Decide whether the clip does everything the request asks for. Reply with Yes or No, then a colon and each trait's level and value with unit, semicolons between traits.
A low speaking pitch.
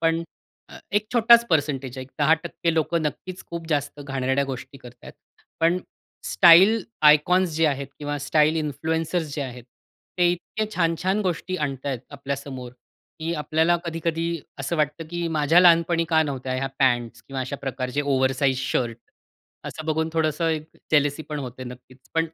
No: medium, 150 Hz